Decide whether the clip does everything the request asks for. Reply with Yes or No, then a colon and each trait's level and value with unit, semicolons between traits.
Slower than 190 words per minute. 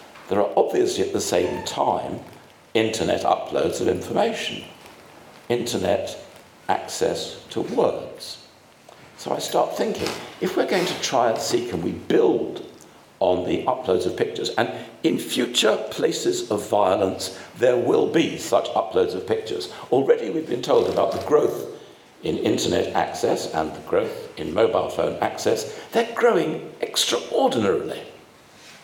Yes: average, 140 wpm